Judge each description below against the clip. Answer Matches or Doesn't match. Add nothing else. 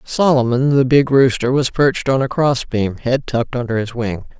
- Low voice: Matches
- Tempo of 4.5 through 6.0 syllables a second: Matches